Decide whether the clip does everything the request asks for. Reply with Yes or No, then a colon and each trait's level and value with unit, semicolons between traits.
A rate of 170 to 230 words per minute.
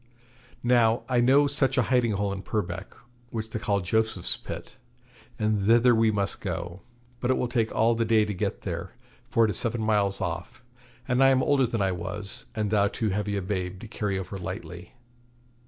Yes: average, 200 wpm